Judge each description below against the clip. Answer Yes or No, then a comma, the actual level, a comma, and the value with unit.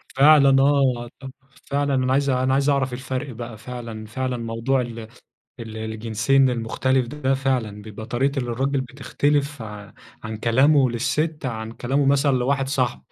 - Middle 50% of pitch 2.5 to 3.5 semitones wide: Yes, average, 3.0 semitones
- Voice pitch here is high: No, low, 130 Hz